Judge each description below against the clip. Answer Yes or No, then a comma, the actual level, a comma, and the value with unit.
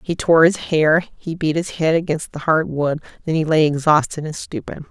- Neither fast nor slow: No, fast, 220 wpm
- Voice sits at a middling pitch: Yes, medium, 160 Hz